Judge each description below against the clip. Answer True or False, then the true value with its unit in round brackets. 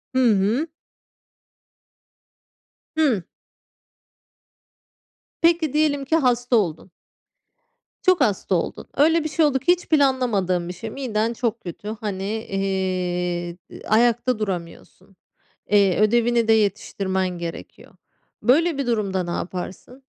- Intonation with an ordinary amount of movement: False (5.8 semitones)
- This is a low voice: False (220 Hz)